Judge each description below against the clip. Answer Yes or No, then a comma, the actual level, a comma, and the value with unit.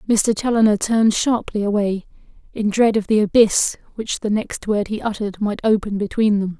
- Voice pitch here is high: Yes, high, 210 Hz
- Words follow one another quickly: No, average, 180 wpm